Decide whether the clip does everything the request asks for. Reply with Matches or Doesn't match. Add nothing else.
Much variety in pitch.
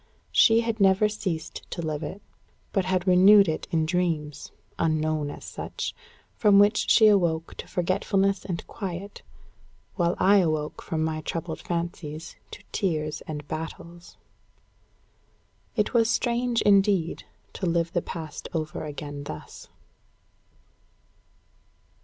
Doesn't match